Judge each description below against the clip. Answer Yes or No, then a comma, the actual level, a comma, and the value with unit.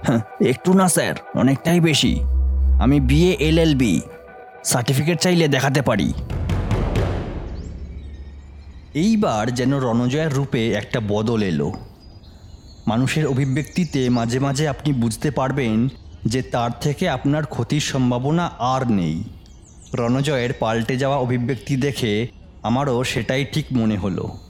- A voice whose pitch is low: Yes, low, 125 Hz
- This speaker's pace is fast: No, average, 110 wpm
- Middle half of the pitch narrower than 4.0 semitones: No, wide, 5.4 semitones